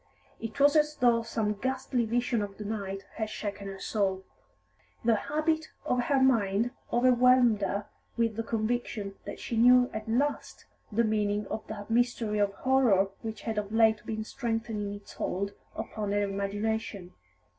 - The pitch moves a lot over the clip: No, average, 3.0 semitones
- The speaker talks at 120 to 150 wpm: No, average, 160 wpm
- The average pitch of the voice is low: No, high, 220 Hz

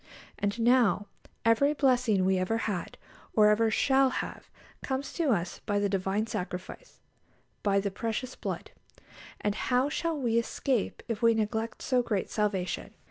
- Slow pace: No, average, 150 wpm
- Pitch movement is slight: No, average, 3.8 semitones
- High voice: Yes, high, 225 Hz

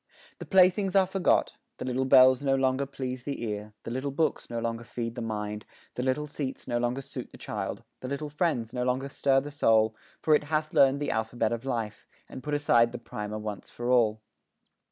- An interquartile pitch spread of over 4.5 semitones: No, average, 3.6 semitones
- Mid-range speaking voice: No, low, 130 Hz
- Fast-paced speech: Yes, fast, 210 wpm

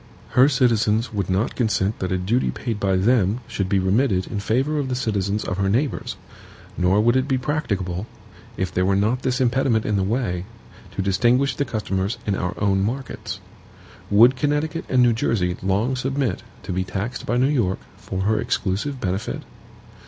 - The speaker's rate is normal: Yes, average, 180 wpm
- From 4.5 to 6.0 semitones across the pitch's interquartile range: Yes, average, 4.9 semitones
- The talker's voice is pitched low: Yes, low, 110 Hz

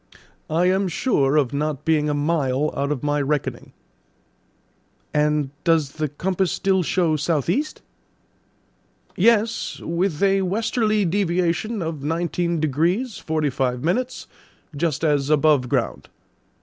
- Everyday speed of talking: No, slow, 125 wpm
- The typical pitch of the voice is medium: Yes, medium, 160 Hz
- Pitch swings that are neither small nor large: Yes, average, 4.2 semitones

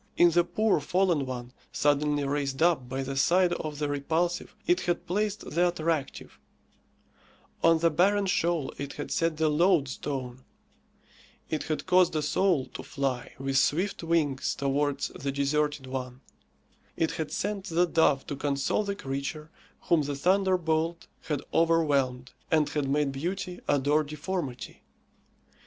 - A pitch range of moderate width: Yes, average, 3.8 semitones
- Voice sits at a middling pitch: Yes, medium, 150 Hz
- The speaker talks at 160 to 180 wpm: No, average, 145 wpm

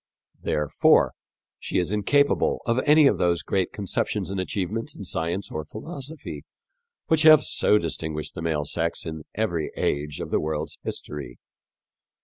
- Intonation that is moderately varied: No, wide, 6.8 semitones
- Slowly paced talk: No, average, 145 wpm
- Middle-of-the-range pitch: No, very low, 90 Hz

